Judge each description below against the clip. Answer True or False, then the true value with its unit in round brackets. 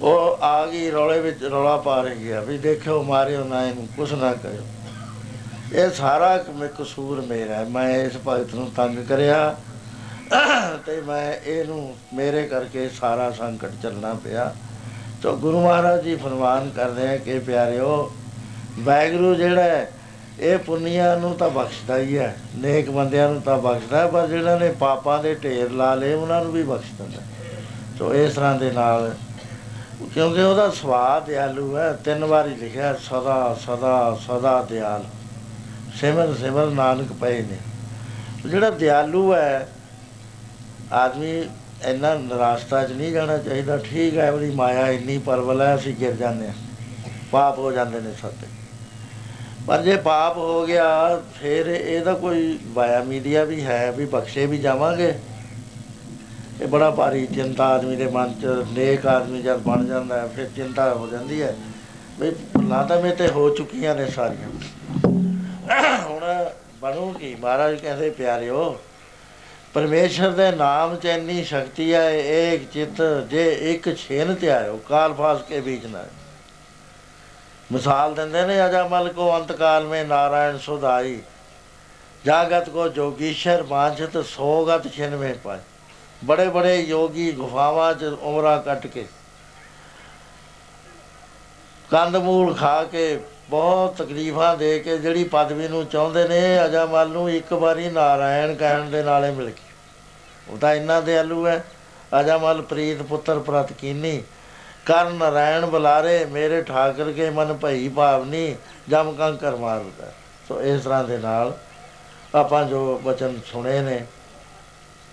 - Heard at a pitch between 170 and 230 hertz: False (140 Hz)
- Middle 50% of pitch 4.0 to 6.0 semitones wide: True (4.5 semitones)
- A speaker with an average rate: True (140 wpm)